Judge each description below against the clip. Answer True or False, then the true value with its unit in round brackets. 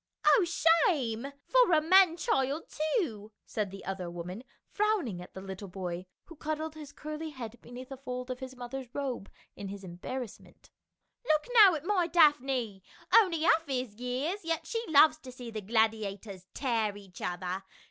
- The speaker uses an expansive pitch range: True (7.5 semitones)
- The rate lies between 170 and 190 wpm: True (180 wpm)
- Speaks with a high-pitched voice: True (255 Hz)